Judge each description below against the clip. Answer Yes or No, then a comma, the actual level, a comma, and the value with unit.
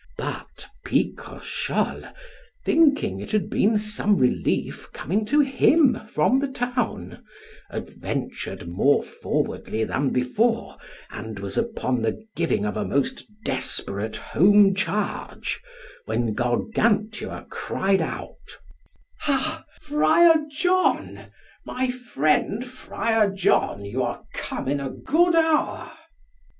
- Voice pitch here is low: No, high, 210 Hz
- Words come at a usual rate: No, slow, 110 wpm